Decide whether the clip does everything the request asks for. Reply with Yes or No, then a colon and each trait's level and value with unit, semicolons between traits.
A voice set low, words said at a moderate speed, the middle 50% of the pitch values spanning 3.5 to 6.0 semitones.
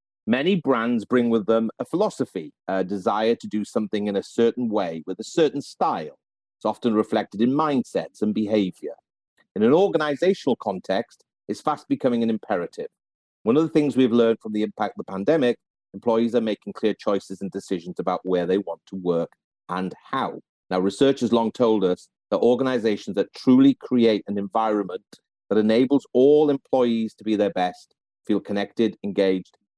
Yes: low, 110 Hz; average, 175 wpm; average, 4.0 semitones